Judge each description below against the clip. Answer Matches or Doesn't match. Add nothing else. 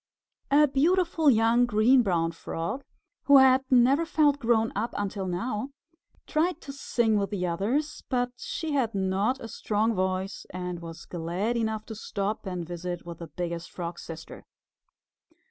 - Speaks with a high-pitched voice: Matches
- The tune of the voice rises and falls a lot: Matches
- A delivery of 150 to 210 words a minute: Matches